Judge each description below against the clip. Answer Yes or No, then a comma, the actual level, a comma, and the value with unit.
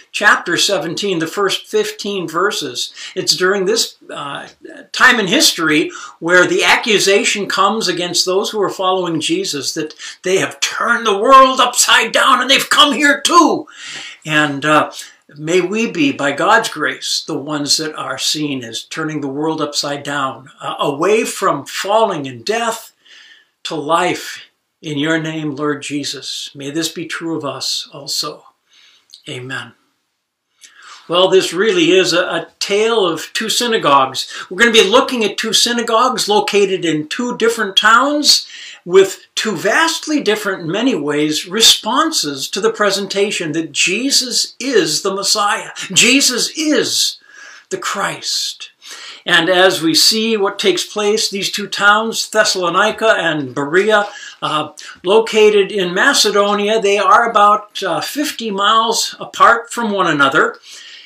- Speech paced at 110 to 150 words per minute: Yes, average, 145 wpm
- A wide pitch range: Yes, wide, 6.4 semitones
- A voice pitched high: Yes, high, 205 Hz